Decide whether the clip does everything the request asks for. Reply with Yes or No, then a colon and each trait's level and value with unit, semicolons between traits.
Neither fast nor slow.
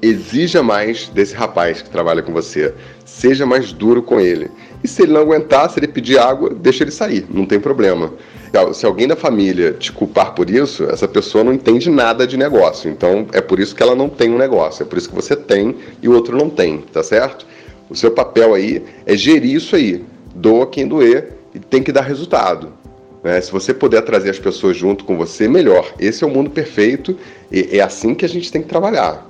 No: fast, 220 wpm